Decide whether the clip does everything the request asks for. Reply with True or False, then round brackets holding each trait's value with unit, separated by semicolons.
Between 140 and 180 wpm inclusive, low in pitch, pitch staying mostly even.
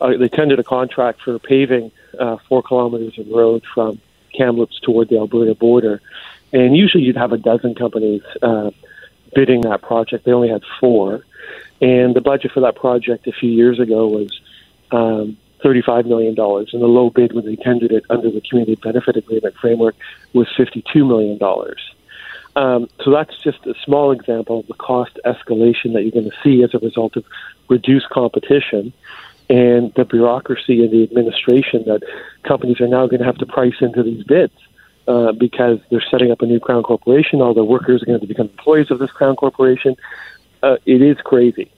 False (190 wpm; 120 Hz; 1.9 semitones)